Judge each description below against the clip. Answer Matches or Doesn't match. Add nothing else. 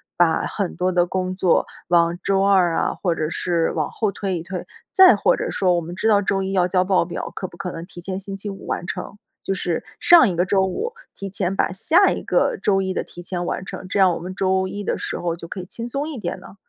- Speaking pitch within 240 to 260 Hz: Doesn't match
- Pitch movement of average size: Doesn't match